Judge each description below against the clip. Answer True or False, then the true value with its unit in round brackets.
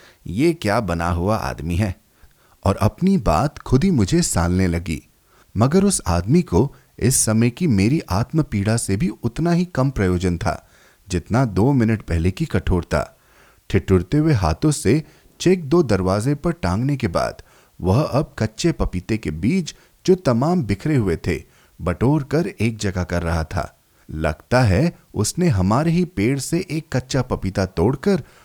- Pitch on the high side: False (110 Hz)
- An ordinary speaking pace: True (160 wpm)